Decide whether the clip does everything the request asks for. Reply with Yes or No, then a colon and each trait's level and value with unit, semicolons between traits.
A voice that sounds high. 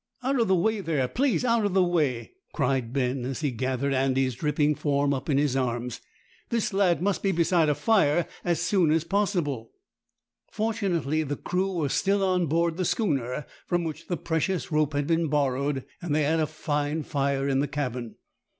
No: medium, 150 Hz